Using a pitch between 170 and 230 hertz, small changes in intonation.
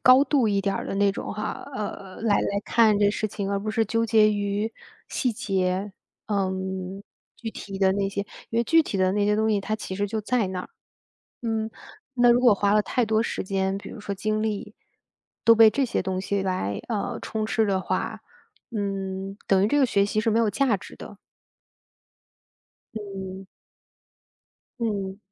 Yes: high, 205 Hz; narrow, 2.2 semitones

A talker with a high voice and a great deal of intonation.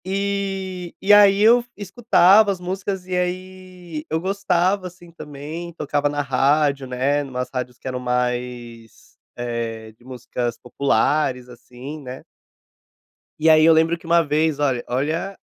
No: medium, 155 Hz; wide, 6.4 semitones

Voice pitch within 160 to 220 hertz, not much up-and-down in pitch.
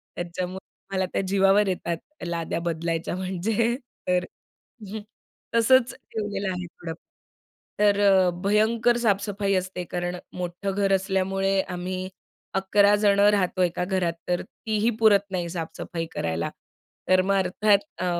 Yes: high, 190 Hz; narrow, 2.2 semitones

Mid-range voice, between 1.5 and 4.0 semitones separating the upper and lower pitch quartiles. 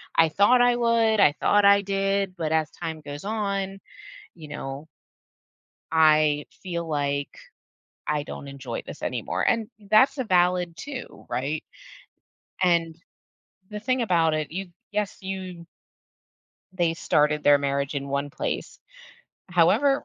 No: medium, 170 Hz; average, 4.9 semitones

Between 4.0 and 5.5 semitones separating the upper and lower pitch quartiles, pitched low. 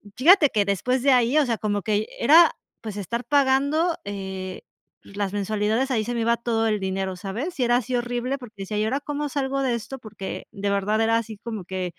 No: average, 4.5 semitones; high, 230 Hz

